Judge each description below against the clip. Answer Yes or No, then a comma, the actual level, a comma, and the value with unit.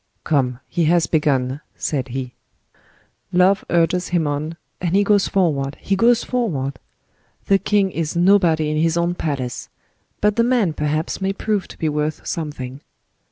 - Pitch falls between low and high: Yes, medium, 165 Hz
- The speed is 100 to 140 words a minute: No, average, 155 wpm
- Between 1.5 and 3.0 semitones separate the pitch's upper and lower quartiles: No, average, 4.8 semitones